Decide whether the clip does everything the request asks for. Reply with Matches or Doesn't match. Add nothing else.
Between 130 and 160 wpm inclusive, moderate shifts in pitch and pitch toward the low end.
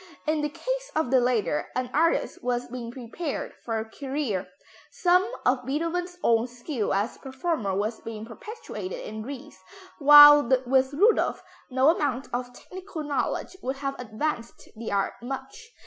Doesn't match